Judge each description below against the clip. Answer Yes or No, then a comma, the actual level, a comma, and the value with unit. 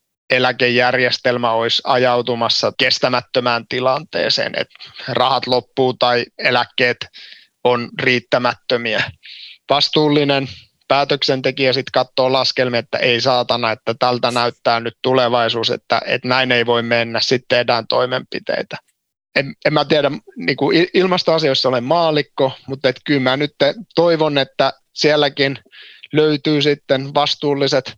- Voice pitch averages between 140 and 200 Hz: No, low, 130 Hz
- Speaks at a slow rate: No, average, 115 wpm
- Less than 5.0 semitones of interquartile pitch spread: Yes, average, 2.8 semitones